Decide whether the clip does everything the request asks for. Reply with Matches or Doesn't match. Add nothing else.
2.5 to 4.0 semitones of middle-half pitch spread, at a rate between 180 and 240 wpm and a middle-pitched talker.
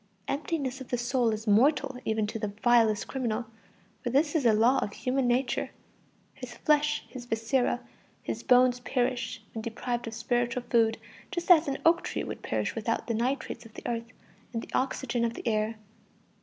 Doesn't match